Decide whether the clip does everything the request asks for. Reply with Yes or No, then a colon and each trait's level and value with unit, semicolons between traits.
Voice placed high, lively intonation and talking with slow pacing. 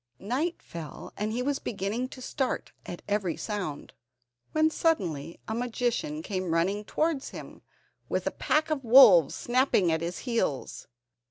No: high, 225 Hz; wide, 7.1 semitones; average, 150 wpm